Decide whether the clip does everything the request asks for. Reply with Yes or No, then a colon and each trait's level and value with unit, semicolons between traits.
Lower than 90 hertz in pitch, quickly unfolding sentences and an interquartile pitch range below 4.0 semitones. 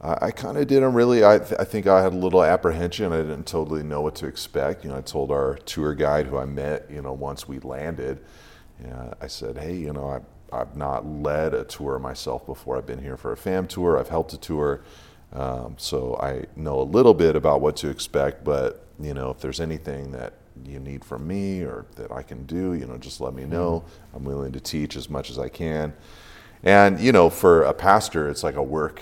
No: very low, 75 Hz; fast, 235 wpm; average, 4.5 semitones